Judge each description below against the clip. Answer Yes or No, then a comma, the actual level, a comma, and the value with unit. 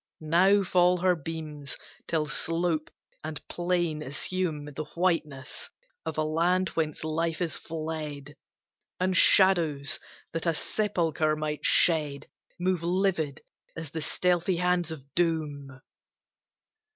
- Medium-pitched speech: Yes, medium, 165 Hz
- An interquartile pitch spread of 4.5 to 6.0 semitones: No, average, 2.7 semitones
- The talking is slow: Yes, slow, 115 wpm